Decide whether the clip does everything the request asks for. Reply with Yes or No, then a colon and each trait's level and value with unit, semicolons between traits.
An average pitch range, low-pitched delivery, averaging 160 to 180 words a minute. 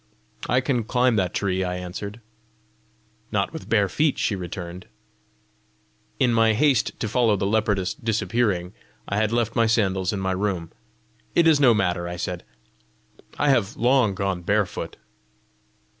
No: average, 4.0 semitones; low, 105 Hz; average, 150 wpm